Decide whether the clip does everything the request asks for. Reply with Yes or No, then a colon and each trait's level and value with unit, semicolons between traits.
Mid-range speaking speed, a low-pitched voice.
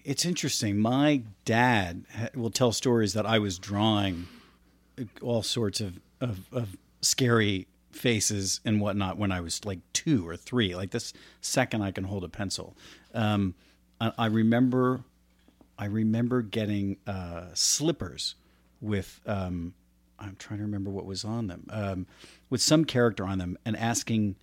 Yes: average, 150 wpm; low, 105 Hz